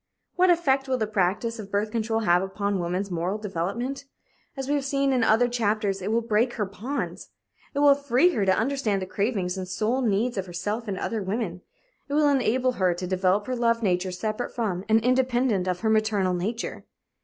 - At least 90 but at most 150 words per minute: No, average, 200 wpm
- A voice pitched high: Yes, high, 215 Hz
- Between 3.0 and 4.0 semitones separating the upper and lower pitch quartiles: No, average, 4.5 semitones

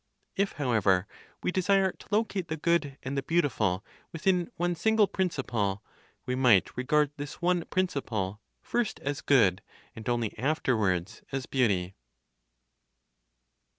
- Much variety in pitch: Yes, wide, 8.1 semitones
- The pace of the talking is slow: Yes, slow, 125 wpm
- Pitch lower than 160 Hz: Yes, medium, 140 Hz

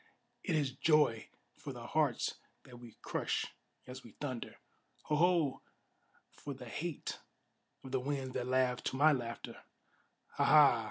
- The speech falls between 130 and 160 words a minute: Yes, average, 150 wpm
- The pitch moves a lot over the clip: No, average, 3.1 semitones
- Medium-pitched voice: No, low, 130 Hz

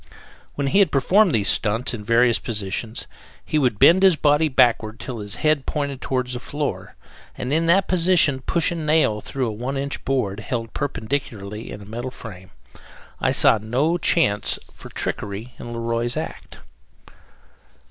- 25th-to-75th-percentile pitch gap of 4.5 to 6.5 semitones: Yes, average, 5.2 semitones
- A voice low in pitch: Yes, low, 125 Hz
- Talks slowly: No, average, 170 wpm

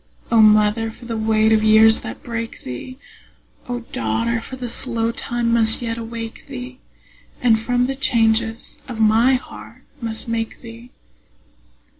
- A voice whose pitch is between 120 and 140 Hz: No, high, 230 Hz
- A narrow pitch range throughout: Yes, narrow, 1.3 semitones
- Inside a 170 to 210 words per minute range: No, average, 145 wpm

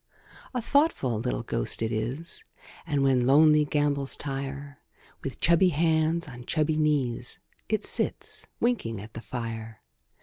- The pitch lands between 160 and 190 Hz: No, medium, 140 Hz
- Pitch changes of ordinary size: Yes, average, 4.6 semitones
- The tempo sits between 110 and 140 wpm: Yes, slow, 135 wpm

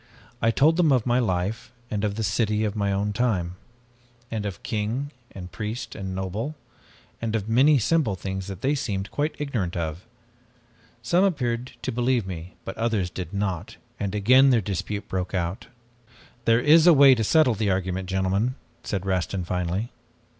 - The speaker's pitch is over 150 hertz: No, low, 105 Hz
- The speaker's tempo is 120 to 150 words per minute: No, average, 175 wpm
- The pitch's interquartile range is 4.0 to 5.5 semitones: Yes, average, 4.6 semitones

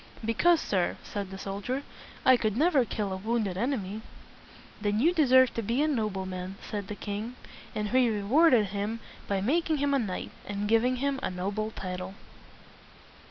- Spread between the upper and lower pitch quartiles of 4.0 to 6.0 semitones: Yes, average, 4.5 semitones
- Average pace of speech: Yes, average, 185 wpm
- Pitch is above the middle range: Yes, high, 215 Hz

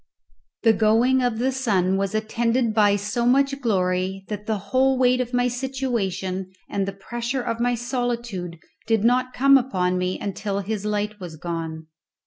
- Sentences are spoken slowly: No, average, 165 wpm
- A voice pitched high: Yes, high, 220 Hz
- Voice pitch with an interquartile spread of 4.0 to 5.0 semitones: Yes, average, 4.3 semitones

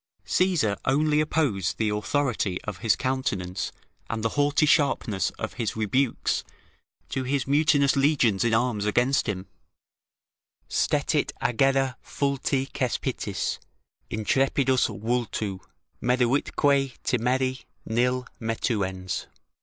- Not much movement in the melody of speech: No, average, 4.0 semitones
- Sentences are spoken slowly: Yes, slow, 100 wpm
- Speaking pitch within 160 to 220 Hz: No, low, 125 Hz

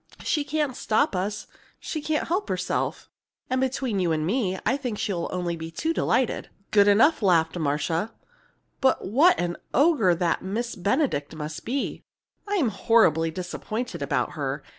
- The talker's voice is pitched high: Yes, high, 210 Hz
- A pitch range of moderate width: No, wide, 7.4 semitones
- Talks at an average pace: Yes, average, 155 wpm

